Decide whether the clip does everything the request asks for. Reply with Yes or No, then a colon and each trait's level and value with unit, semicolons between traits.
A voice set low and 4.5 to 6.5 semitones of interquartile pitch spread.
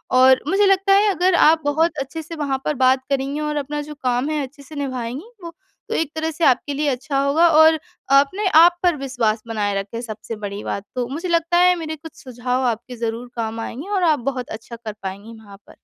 No: very high, 275 Hz; average, 4.9 semitones